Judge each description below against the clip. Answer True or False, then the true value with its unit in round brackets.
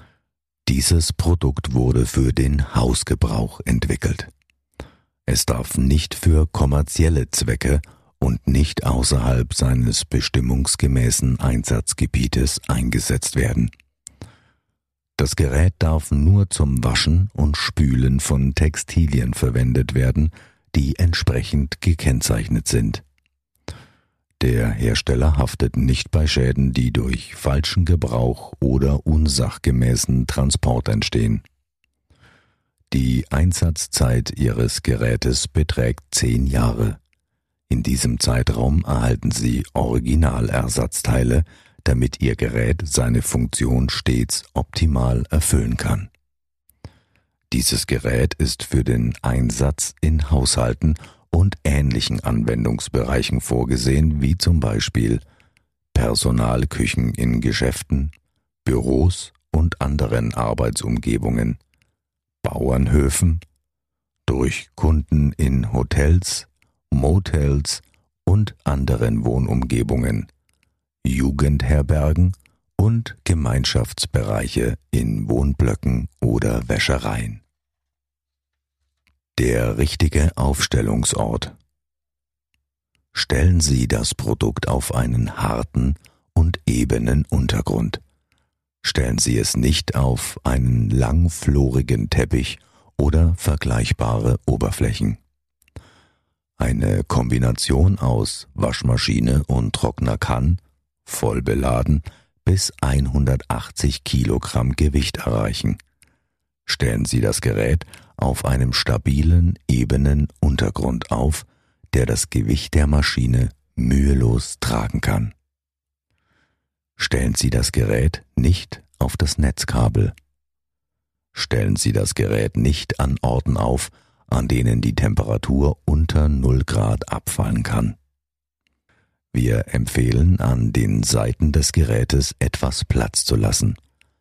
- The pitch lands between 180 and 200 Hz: False (70 Hz)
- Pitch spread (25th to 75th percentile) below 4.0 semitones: False (4.6 semitones)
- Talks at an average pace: False (90 wpm)